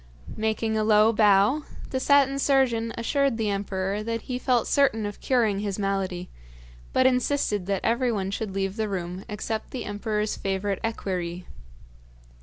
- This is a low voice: No, high, 215 Hz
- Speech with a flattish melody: No, average, 3.2 semitones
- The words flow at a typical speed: Yes, average, 150 wpm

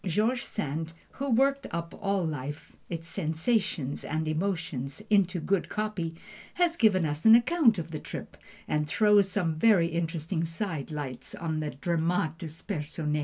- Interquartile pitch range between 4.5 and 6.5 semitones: Yes, average, 4.9 semitones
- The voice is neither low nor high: Yes, medium, 170 Hz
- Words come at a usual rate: Yes, average, 150 wpm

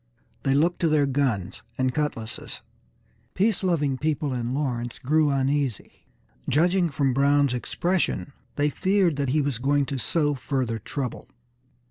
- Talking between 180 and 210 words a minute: No, average, 140 wpm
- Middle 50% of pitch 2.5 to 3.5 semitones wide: Yes, average, 2.9 semitones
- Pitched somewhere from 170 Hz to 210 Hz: No, medium, 140 Hz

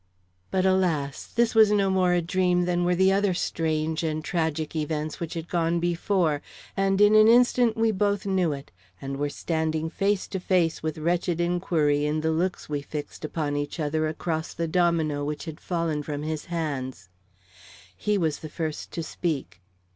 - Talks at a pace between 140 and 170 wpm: No, average, 180 wpm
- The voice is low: No, medium, 165 Hz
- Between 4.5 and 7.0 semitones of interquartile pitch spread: No, average, 3.2 semitones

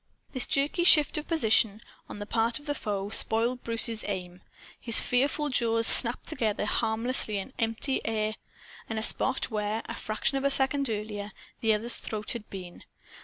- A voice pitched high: Yes, high, 225 Hz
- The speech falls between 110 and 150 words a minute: No, average, 170 wpm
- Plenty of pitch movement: No, average, 3.5 semitones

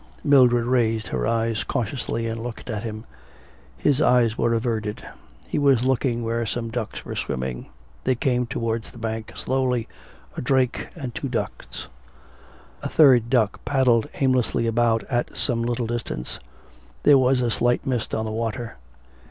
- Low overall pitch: Yes, low, 120 Hz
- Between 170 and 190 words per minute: No, average, 155 wpm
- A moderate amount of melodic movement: No, narrow, 2.1 semitones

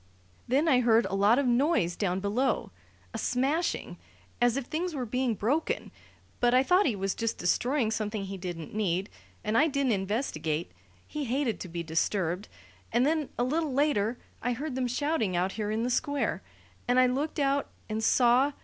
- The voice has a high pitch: Yes, high, 245 Hz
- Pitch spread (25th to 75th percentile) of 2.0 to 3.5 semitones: No, average, 5.2 semitones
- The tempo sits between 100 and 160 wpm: No, average, 185 wpm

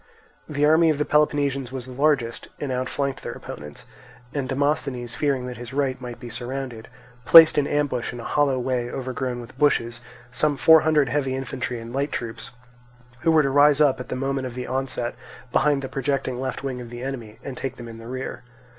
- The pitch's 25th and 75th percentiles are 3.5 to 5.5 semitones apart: No, average, 2.7 semitones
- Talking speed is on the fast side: Yes, fast, 210 wpm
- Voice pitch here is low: Yes, low, 130 Hz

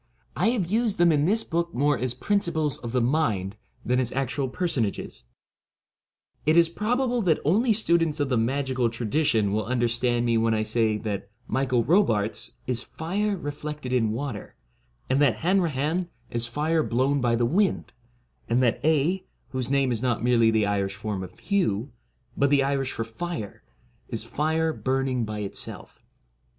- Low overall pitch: Yes, low, 130 Hz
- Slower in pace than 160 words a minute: No, average, 170 wpm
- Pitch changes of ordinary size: No, wide, 5.8 semitones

